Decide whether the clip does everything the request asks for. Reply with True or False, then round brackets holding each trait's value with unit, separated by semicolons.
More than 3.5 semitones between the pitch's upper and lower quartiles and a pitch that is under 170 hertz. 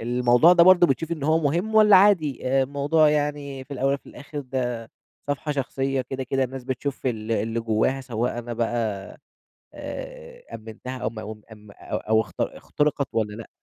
True (4.2 semitones; 135 Hz)